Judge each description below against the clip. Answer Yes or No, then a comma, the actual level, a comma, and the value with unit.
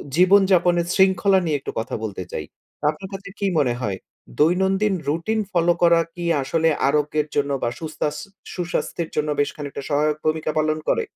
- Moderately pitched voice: Yes, medium, 160 Hz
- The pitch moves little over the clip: No, average, 3.8 semitones